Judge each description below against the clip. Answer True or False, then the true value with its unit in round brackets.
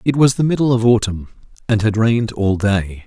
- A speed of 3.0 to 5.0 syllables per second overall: False (5.4 syllables/s)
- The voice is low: True (110 Hz)